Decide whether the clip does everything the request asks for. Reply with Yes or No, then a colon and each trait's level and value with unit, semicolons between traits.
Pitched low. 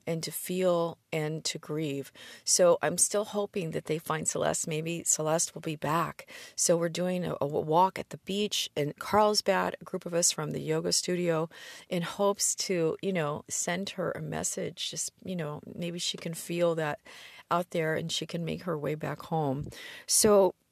No: medium, 170 Hz